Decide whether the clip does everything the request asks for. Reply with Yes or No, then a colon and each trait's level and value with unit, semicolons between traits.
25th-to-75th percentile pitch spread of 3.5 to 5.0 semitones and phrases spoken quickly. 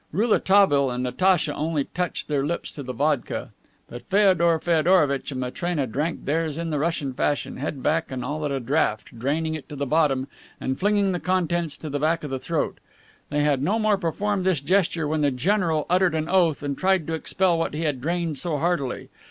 Yes: average, 3.8 semitones; fast, 210 wpm